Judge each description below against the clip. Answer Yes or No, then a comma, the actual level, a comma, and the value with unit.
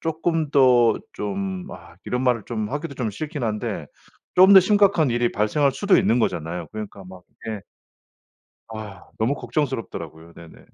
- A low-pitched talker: Yes, low, 120 Hz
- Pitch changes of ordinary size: No, wide, 6.6 semitones